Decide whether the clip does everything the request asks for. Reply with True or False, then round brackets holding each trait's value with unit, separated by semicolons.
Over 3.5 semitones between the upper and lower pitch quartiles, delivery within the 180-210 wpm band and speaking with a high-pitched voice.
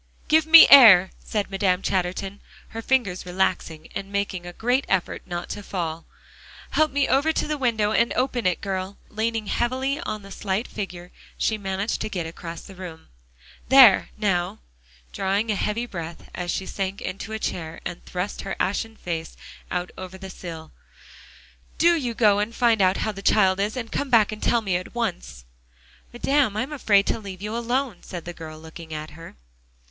True (4.3 semitones; 185 wpm; 200 Hz)